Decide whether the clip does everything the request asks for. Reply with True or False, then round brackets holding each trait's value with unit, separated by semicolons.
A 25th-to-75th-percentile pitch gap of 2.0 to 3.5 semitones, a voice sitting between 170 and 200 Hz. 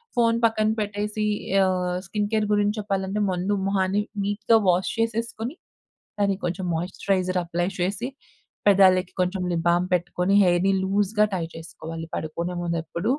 True (2.6 semitones; 190 Hz)